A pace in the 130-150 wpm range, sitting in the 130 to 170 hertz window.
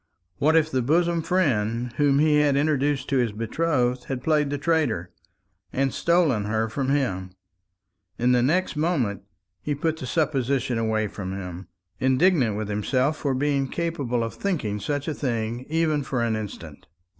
No: average, 165 wpm; low, 135 Hz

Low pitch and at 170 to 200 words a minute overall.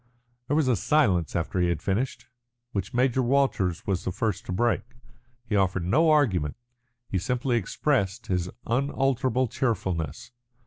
No: low, 115 Hz; average, 150 wpm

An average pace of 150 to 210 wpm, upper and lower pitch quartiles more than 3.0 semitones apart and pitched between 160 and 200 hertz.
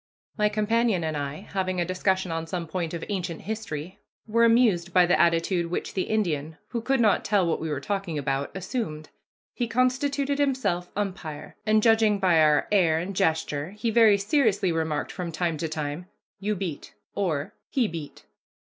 Yes: average, 175 wpm; average, 4.8 semitones; medium, 185 Hz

